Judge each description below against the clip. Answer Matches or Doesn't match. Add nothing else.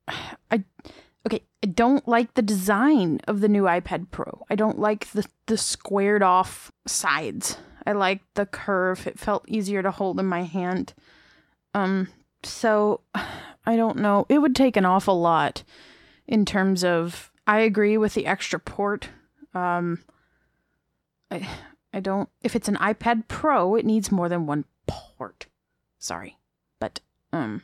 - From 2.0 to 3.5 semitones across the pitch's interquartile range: Matches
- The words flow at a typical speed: Matches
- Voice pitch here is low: Doesn't match